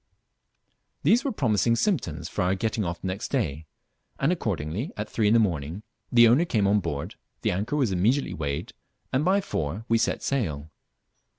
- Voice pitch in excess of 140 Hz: No, low, 105 Hz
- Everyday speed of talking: Yes, average, 180 wpm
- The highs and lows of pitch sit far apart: Yes, wide, 6.7 semitones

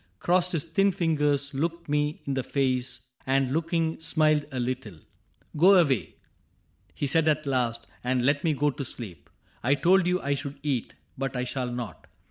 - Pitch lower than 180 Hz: Yes, medium, 140 Hz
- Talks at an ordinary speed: Yes, average, 185 wpm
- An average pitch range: Yes, average, 3.8 semitones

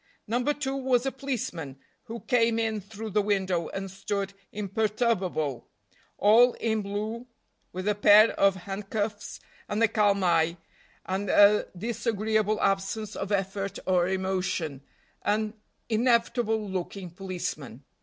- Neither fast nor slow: No, slow, 125 wpm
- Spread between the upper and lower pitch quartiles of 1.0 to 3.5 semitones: Yes, average, 2.7 semitones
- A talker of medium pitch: No, high, 205 Hz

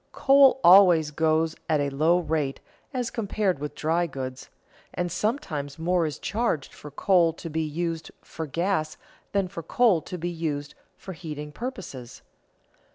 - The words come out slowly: No, average, 155 wpm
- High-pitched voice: No, medium, 165 Hz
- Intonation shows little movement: No, average, 3.7 semitones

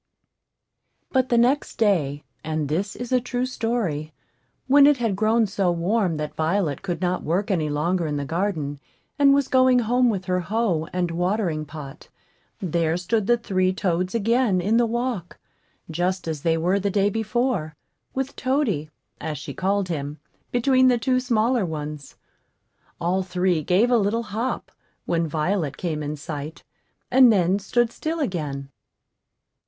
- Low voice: No, high, 190 Hz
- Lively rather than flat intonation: Yes, wide, 6.5 semitones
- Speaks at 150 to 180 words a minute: Yes, average, 160 wpm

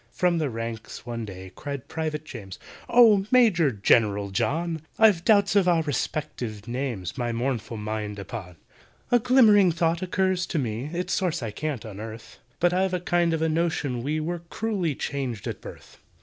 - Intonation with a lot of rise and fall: Yes, wide, 7.6 semitones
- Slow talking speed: No, average, 170 wpm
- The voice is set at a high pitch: No, medium, 150 Hz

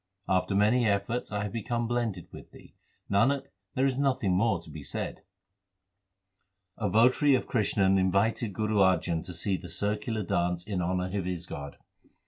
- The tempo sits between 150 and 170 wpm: Yes, average, 165 wpm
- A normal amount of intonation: Yes, average, 4.0 semitones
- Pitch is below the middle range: Yes, low, 100 Hz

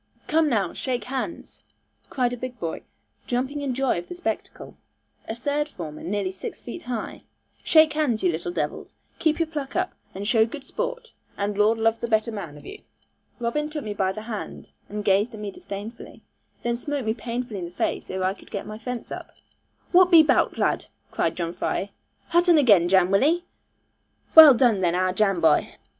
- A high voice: Yes, high, 230 Hz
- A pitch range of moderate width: No, wide, 6.5 semitones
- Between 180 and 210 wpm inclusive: Yes, average, 200 wpm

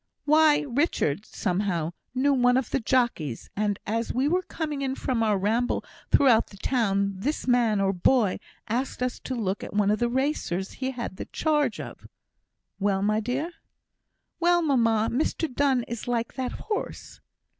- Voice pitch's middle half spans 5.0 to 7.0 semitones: No, average, 4.6 semitones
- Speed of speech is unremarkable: Yes, average, 165 wpm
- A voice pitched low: No, high, 240 Hz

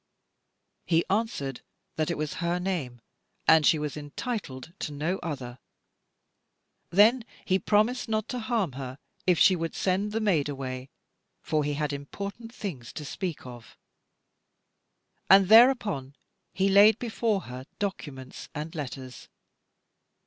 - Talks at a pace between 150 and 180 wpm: No, slow, 135 wpm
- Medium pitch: Yes, medium, 165 Hz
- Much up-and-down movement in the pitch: Yes, wide, 6.5 semitones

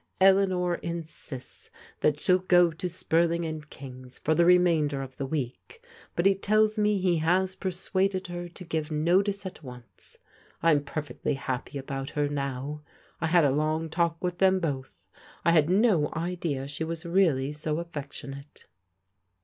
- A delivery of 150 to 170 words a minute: Yes, average, 155 wpm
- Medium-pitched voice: Yes, medium, 165 Hz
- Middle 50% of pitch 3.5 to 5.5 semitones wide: Yes, average, 3.8 semitones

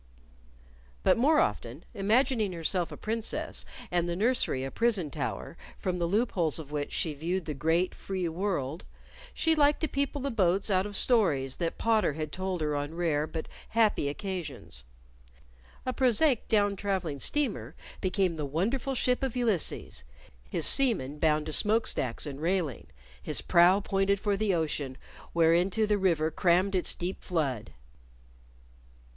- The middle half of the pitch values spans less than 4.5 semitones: No, wide, 5.5 semitones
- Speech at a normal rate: Yes, average, 155 wpm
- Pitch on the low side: No, medium, 185 Hz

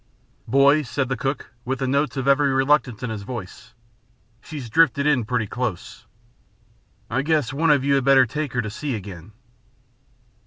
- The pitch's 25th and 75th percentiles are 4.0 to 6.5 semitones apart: No, average, 3.0 semitones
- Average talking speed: Yes, average, 170 wpm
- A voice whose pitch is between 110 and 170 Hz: Yes, low, 135 Hz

